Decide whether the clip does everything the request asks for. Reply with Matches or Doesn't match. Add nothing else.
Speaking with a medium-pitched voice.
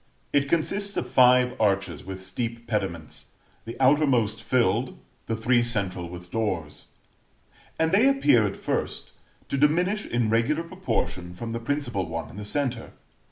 Doesn't match